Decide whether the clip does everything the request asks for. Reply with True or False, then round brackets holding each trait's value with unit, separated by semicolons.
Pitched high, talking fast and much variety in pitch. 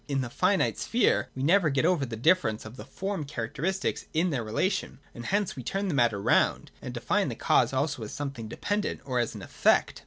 False (140 Hz; 215 wpm; 7.5 semitones)